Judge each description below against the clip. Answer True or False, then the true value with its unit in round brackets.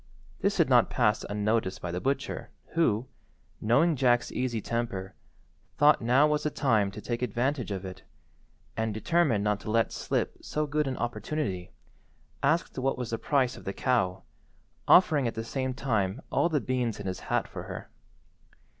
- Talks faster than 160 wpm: True (170 wpm)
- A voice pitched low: True (120 Hz)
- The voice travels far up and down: False (4.6 semitones)